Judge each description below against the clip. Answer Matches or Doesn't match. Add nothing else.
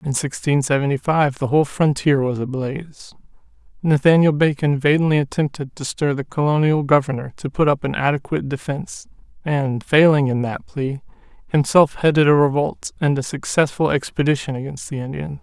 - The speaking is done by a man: Matches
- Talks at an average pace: Matches